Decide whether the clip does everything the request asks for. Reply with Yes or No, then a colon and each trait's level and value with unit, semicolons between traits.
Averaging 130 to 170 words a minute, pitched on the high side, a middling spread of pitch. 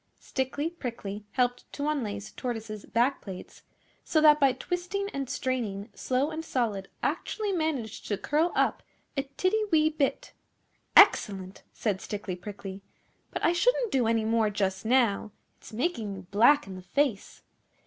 No: average, 150 wpm; high, 245 Hz; wide, 6.5 semitones